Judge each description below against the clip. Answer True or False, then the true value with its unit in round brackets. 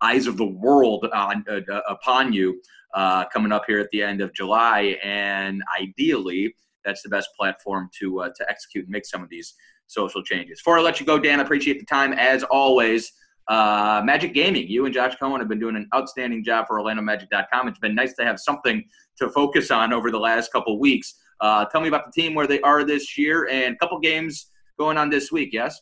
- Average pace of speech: False (225 wpm)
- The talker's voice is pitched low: True (125 Hz)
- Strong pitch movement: True (5.9 semitones)